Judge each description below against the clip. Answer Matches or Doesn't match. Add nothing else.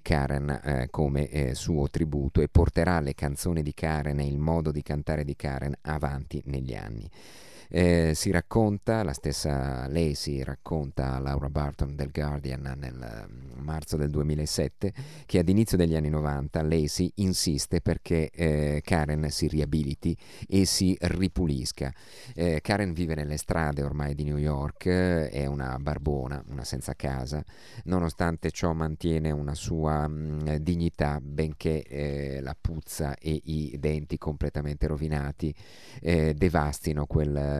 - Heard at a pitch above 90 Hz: Doesn't match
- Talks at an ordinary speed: Matches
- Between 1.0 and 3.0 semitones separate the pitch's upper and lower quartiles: Matches